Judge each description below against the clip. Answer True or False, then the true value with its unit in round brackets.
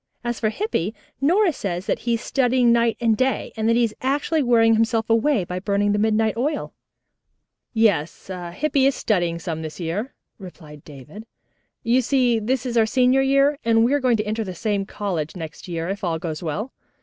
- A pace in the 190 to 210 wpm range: True (195 wpm)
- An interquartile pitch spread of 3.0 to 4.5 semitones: False (5.2 semitones)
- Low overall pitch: False (225 Hz)